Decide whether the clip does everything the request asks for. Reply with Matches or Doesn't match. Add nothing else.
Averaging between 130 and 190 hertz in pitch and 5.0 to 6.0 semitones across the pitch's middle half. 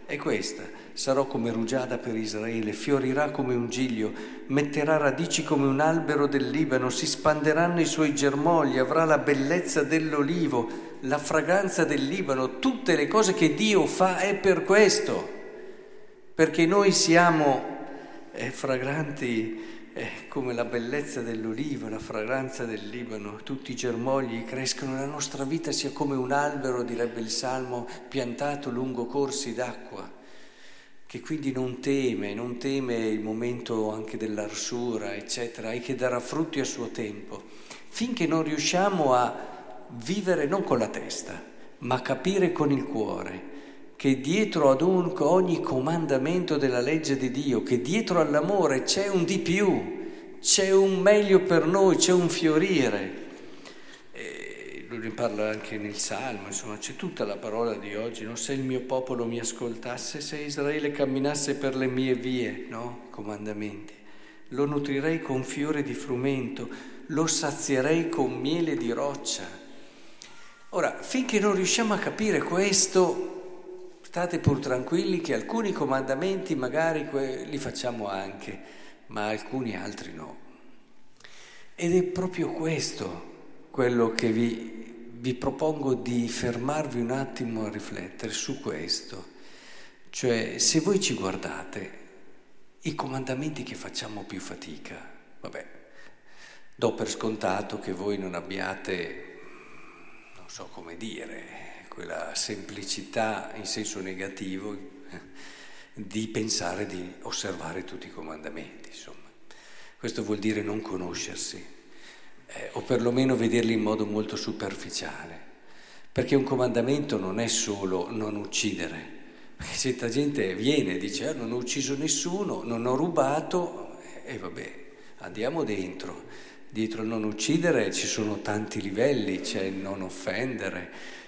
Matches